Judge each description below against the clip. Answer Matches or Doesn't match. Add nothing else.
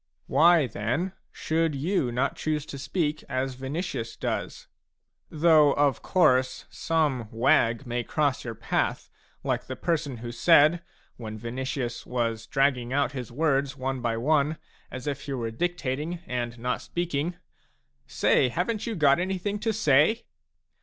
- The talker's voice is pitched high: Doesn't match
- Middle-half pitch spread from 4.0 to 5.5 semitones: Matches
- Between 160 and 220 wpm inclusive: Doesn't match